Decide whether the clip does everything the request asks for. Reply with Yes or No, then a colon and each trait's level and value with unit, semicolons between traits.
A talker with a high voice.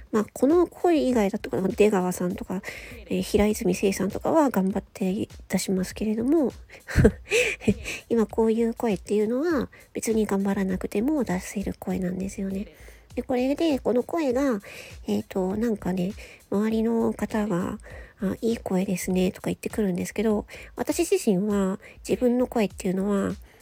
Yes: high, 210 Hz